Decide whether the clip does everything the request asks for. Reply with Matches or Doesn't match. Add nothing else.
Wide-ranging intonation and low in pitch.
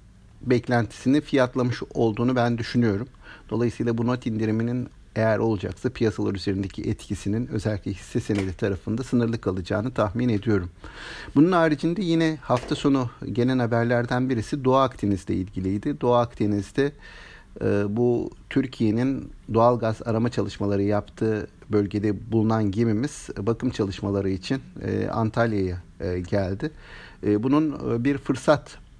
Doesn't match